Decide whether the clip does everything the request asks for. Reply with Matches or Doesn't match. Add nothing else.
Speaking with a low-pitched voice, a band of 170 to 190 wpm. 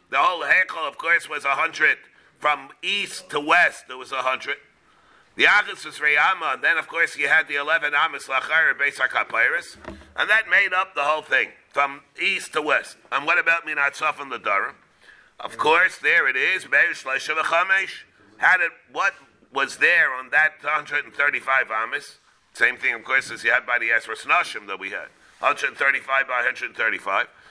Doesn't match